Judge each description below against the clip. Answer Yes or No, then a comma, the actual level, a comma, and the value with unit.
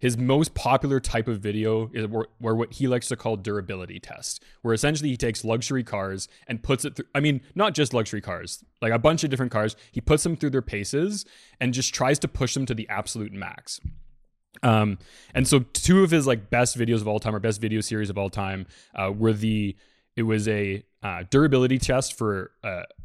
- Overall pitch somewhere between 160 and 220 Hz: No, low, 115 Hz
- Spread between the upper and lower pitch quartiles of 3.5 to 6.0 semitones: Yes, average, 4.1 semitones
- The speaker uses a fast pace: Yes, fast, 215 wpm